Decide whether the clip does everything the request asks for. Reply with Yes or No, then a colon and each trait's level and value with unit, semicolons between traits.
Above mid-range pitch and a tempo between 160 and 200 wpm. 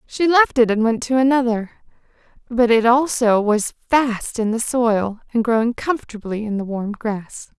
Yes: high, 235 Hz; average, 175 wpm